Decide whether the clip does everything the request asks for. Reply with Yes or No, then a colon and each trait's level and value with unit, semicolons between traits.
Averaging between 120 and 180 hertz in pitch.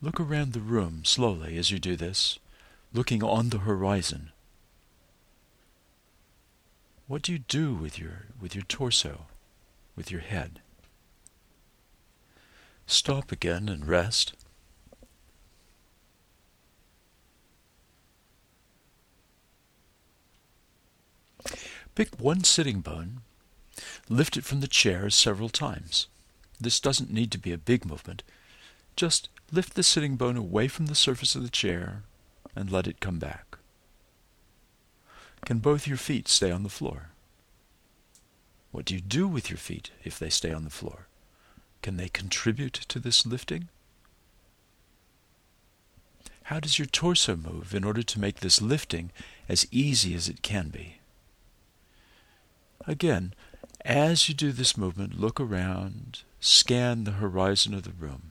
No: low, 100 Hz